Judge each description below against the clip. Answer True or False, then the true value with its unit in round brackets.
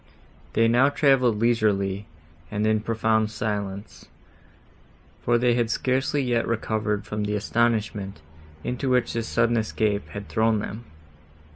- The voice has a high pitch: False (110 Hz)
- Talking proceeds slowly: True (130 wpm)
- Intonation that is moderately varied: False (2.2 semitones)